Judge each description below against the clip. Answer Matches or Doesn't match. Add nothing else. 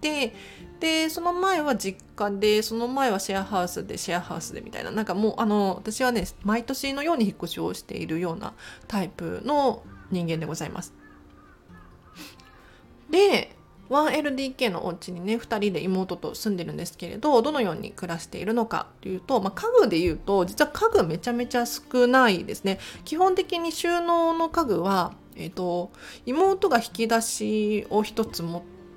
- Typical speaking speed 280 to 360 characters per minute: Matches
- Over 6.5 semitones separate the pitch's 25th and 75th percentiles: Matches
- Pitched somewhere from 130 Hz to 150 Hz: Doesn't match